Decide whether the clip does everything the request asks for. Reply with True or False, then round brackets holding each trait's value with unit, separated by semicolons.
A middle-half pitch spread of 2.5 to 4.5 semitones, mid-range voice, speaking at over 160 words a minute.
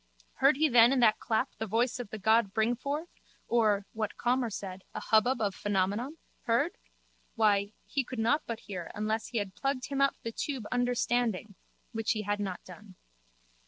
False (3.3 semitones; 225 Hz; 180 wpm)